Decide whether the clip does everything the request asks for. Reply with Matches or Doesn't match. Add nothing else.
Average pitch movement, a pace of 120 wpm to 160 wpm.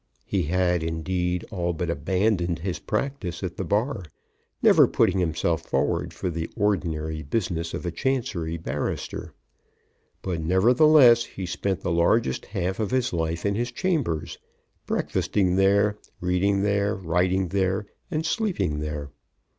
Matches